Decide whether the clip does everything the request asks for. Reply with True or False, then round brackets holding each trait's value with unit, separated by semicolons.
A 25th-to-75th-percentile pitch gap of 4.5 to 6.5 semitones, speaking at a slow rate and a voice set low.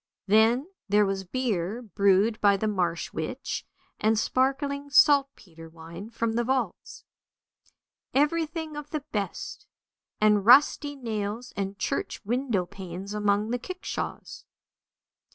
False (5.1 semitones; 115 wpm; 220 Hz)